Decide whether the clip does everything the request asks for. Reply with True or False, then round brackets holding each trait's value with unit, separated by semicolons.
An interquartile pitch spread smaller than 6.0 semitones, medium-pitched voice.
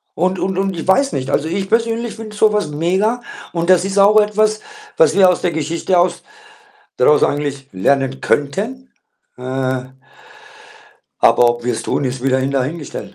False (7.4 semitones; 175 Hz)